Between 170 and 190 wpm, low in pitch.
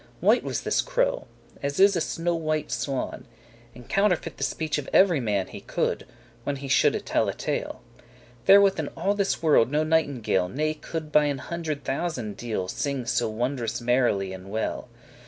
No: average, 180 wpm; medium, 145 Hz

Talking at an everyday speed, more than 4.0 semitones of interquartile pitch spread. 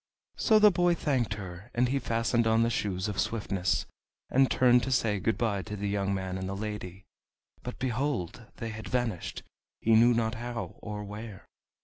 No: average, 190 wpm; average, 3.4 semitones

